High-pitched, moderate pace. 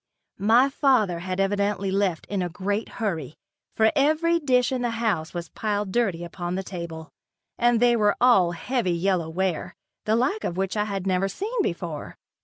Yes: high, 200 Hz; average, 180 wpm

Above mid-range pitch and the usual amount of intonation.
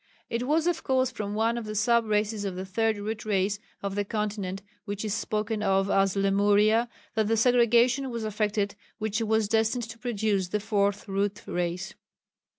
No: high, 215 Hz; narrow, 2.1 semitones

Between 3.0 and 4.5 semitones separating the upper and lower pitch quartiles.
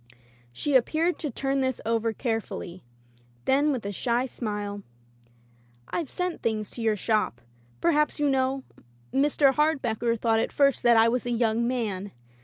Yes: average, 3.8 semitones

